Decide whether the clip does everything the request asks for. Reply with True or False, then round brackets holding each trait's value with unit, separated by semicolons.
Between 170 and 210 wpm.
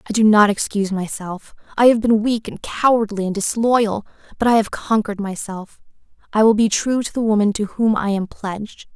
True (190 wpm)